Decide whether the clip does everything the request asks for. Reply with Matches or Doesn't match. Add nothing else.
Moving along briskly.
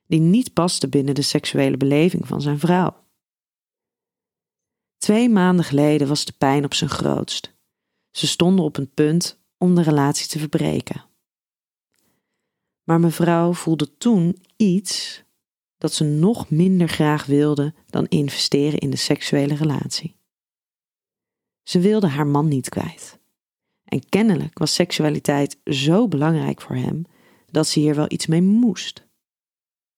Doesn't match